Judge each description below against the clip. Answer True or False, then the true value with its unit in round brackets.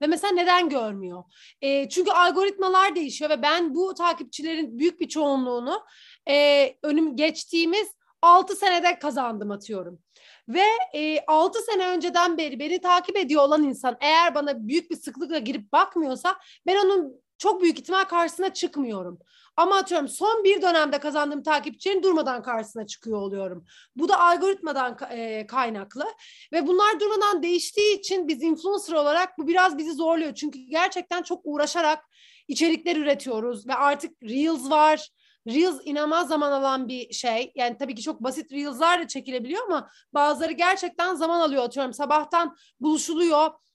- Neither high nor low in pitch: False (315 Hz)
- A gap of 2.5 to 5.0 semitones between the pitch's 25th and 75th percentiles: True (4.3 semitones)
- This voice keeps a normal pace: False (145 wpm)